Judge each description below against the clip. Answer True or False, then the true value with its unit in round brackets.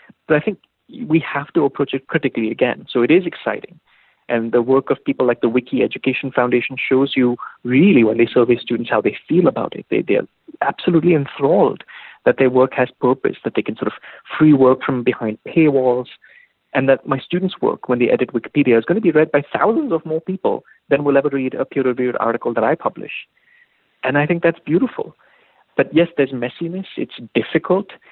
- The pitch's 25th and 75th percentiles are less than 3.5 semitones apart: False (4.3 semitones)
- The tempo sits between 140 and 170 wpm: False (205 wpm)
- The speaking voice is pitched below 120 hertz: False (135 Hz)